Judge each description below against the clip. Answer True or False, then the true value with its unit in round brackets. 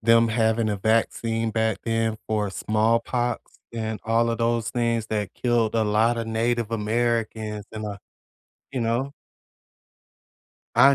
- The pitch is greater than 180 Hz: False (115 Hz)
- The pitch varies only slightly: True (1.1 semitones)